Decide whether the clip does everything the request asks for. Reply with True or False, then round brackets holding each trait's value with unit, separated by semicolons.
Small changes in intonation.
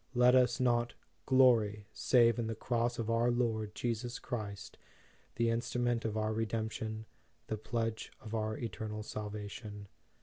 True (1.9 semitones)